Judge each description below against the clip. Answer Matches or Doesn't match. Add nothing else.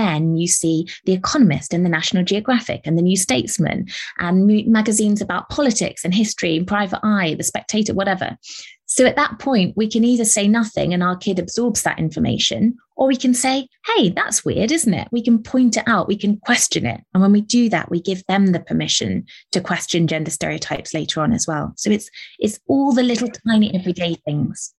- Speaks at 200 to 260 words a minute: Matches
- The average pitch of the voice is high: Matches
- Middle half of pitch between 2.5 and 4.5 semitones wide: Doesn't match